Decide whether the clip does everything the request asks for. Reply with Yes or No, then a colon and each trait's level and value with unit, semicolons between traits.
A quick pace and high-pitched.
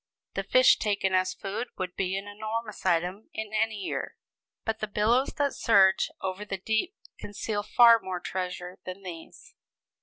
No: average, 160 wpm; high, 205 Hz